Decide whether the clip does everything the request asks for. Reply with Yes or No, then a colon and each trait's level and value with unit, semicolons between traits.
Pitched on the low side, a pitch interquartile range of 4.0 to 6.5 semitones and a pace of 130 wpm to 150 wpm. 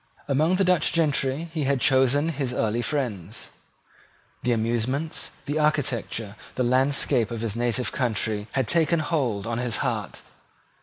Yes: low, 130 Hz; average, 4.3 semitones; average, 145 wpm